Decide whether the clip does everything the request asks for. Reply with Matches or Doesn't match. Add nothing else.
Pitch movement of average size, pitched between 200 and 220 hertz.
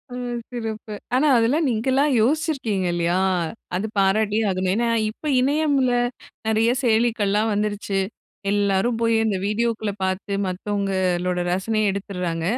Matches